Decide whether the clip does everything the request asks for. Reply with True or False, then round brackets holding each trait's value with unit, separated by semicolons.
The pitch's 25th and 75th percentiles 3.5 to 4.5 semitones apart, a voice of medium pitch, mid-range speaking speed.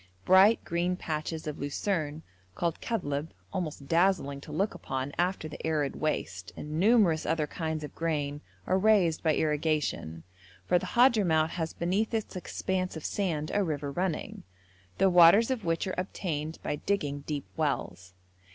True (3.9 semitones; 160 Hz; 155 wpm)